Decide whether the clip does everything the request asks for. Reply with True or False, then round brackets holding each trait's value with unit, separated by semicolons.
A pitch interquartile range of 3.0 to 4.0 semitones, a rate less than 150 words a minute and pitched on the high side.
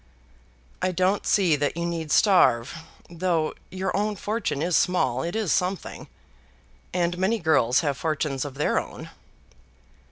False (3.7 semitones; 140 wpm; 170 Hz)